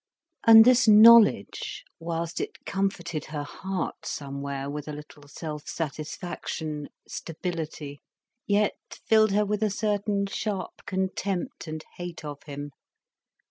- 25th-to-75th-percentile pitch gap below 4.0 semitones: No, average, 5.3 semitones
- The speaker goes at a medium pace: No, slow, 120 wpm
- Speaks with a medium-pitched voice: Yes, medium, 170 Hz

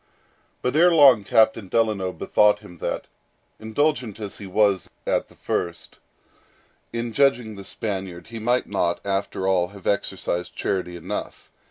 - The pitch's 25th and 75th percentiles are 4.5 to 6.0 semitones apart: No, average, 3.4 semitones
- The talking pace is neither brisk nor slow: Yes, average, 145 wpm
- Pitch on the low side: Yes, low, 105 Hz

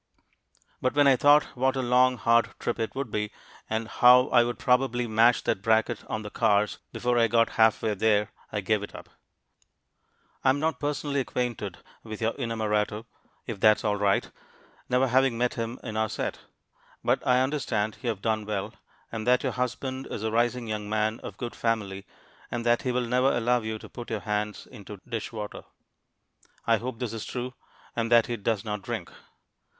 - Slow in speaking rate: No, average, 190 wpm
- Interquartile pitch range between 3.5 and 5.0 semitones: No, narrow, 2.6 semitones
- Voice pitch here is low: Yes, low, 115 Hz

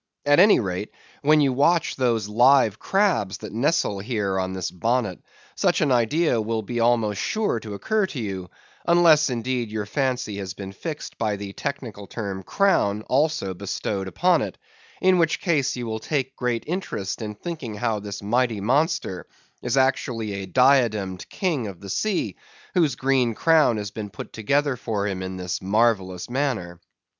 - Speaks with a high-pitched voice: No, low, 115 Hz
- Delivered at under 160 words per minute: No, average, 170 wpm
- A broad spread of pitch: Yes, wide, 5.8 semitones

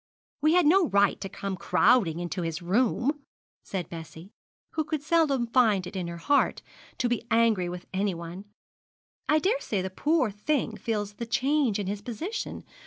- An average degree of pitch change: No, wide, 7.3 semitones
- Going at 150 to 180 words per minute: Yes, average, 170 wpm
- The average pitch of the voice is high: Yes, high, 215 Hz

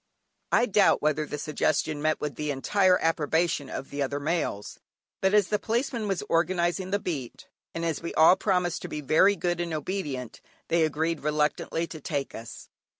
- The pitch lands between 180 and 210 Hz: No, medium, 165 Hz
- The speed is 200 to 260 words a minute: No, average, 180 wpm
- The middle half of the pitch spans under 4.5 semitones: Yes, average, 3.6 semitones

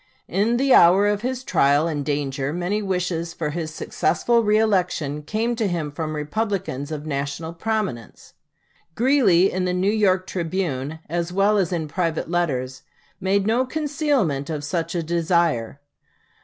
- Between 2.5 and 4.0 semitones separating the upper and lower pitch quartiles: No, average, 5.2 semitones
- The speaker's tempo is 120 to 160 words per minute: Yes, average, 150 wpm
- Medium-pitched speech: Yes, medium, 175 Hz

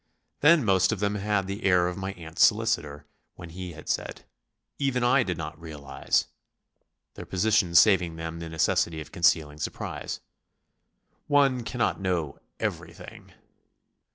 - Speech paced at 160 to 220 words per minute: No, average, 140 wpm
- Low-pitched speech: Yes, very low, 90 Hz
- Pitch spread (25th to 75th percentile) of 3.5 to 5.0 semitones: Yes, average, 4.7 semitones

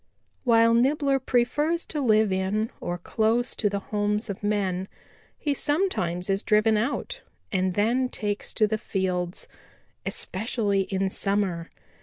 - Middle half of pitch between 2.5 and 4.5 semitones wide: Yes, average, 3.9 semitones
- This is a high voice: Yes, high, 210 Hz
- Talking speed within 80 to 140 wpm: Yes, slow, 135 wpm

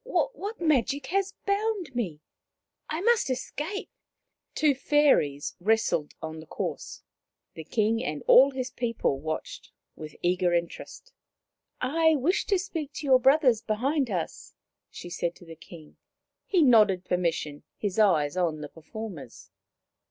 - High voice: Yes, high, 230 Hz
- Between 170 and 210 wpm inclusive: No, average, 145 wpm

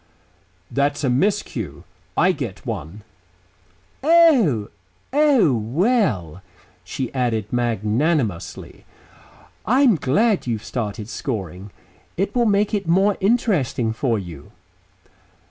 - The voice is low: Yes, low, 130 Hz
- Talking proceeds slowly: Yes, slow, 95 wpm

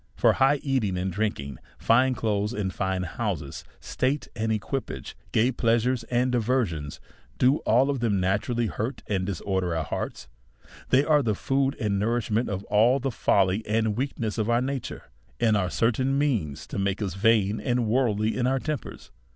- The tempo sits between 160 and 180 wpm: Yes, average, 175 wpm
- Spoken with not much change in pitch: No, average, 4.3 semitones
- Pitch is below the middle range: Yes, low, 110 Hz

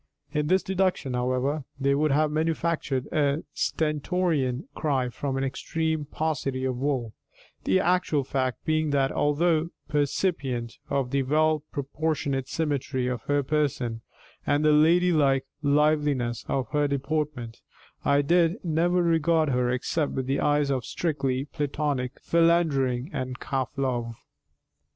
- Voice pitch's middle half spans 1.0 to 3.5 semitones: Yes, average, 3.1 semitones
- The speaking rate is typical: No, slow, 130 wpm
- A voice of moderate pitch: Yes, medium, 145 Hz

